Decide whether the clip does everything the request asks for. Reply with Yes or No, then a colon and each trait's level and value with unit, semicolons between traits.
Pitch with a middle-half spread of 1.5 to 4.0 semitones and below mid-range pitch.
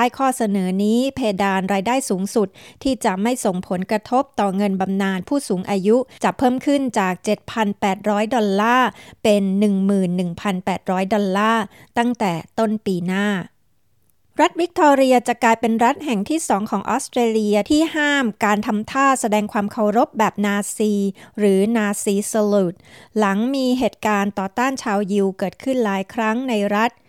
No: average, 3.3 semitones; high, 215 Hz